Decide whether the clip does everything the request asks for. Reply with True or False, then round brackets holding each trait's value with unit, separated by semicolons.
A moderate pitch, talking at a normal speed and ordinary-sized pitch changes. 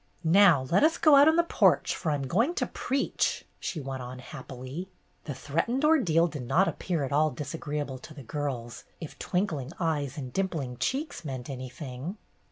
False (150 Hz; 175 wpm; 6.3 semitones)